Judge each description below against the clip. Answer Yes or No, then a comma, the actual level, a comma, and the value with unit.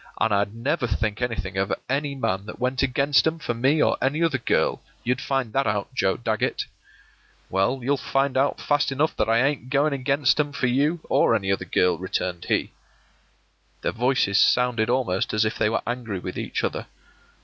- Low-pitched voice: Yes, low, 125 Hz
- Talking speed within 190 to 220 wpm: Yes, average, 195 wpm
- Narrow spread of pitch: No, average, 4.5 semitones